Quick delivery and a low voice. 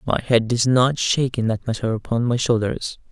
Yes: fast, 210 wpm; low, 120 Hz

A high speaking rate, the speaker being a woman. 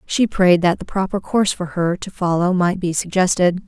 Yes: fast, 210 wpm; female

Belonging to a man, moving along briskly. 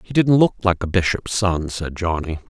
Yes: male; fast, 210 wpm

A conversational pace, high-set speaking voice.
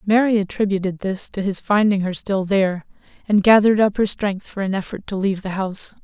No: fast, 210 wpm; high, 195 Hz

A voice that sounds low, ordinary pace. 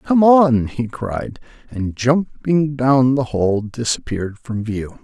Yes: low, 125 Hz; average, 145 wpm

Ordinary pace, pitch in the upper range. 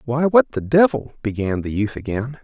No: average, 195 wpm; low, 115 Hz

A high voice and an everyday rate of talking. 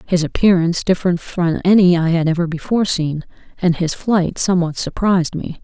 No: medium, 175 Hz; average, 170 wpm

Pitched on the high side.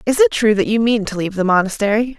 Yes: high, 215 Hz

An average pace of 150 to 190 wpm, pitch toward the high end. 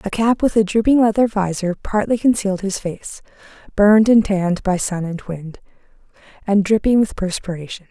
Yes: average, 165 wpm; high, 200 Hz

